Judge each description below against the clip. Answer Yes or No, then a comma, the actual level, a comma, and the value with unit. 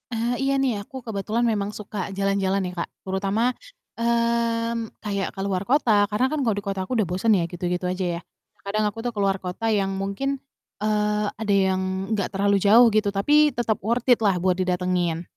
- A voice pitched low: No, high, 205 Hz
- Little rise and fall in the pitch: No, average, 3.2 semitones